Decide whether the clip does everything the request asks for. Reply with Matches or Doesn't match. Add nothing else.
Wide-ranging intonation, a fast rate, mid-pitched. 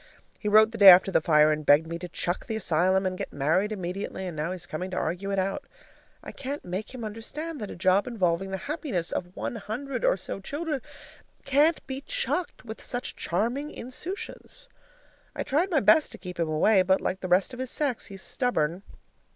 Doesn't match